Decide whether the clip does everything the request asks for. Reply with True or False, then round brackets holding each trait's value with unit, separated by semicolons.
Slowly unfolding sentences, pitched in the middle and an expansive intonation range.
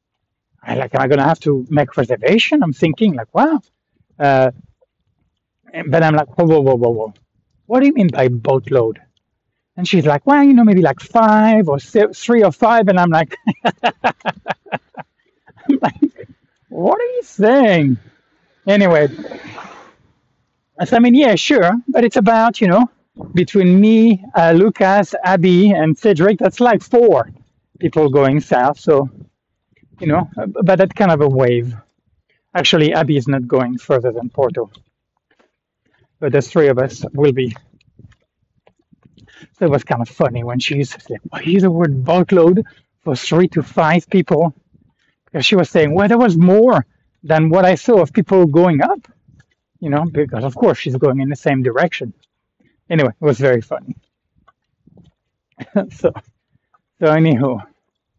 False (160 wpm; 165 Hz; 6.9 semitones)